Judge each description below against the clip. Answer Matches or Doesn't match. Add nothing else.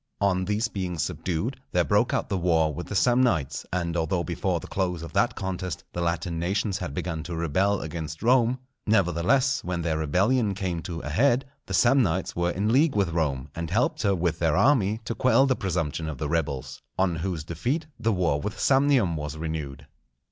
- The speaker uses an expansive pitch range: Doesn't match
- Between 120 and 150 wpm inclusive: Doesn't match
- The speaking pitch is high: Doesn't match